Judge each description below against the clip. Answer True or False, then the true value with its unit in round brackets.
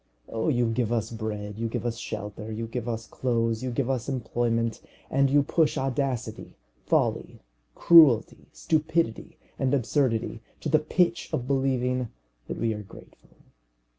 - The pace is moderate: True (150 wpm)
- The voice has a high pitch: False (120 Hz)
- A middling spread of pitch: True (3.3 semitones)